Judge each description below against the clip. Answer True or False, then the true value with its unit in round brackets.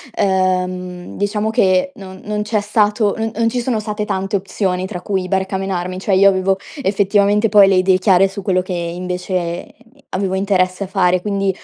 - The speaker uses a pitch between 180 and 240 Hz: True (190 Hz)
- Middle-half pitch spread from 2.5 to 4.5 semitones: False (1.9 semitones)